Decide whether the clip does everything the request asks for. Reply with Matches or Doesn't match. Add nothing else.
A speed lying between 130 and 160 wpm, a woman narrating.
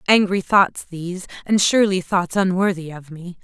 Matches